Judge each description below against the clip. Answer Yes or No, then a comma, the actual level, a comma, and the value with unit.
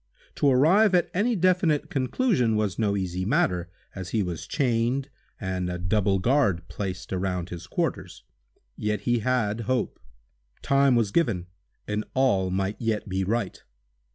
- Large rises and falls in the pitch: Yes, wide, 6.1 semitones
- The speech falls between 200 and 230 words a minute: No, average, 145 wpm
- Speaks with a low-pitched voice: Yes, low, 105 Hz